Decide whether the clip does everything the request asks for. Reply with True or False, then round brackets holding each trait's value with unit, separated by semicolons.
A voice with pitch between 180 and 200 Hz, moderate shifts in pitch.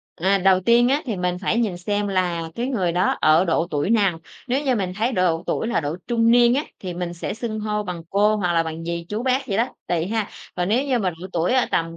True (195 Hz; 5.0 semitones)